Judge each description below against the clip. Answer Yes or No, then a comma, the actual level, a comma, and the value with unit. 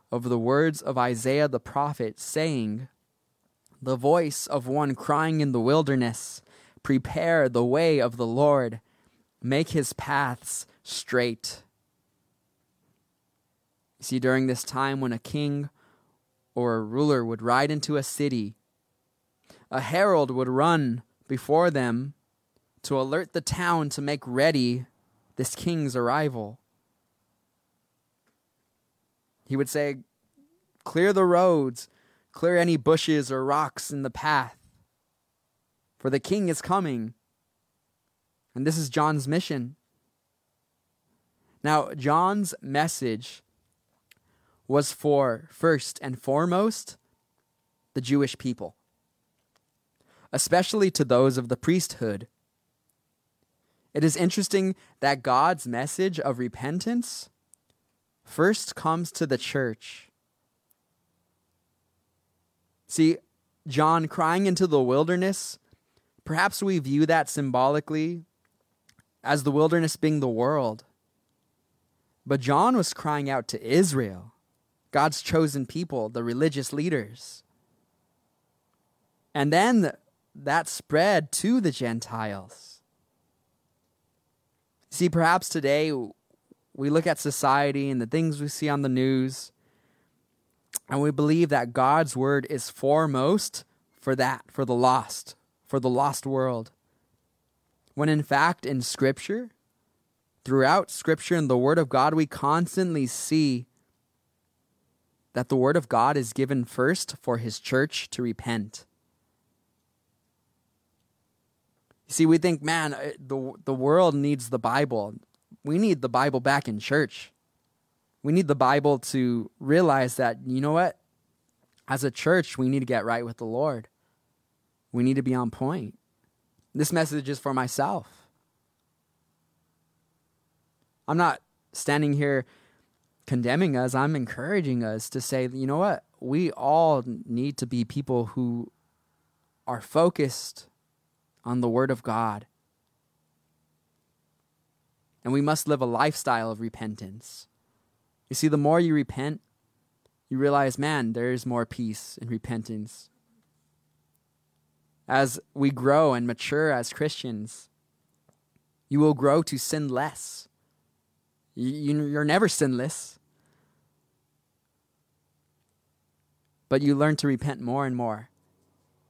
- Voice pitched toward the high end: No, low, 135 Hz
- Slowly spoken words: Yes, slow, 120 wpm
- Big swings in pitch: No, average, 4.1 semitones